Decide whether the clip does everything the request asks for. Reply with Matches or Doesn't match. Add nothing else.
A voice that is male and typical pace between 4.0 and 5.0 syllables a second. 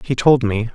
Matches